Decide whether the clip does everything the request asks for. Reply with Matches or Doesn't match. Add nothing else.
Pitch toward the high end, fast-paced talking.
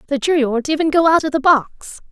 Matches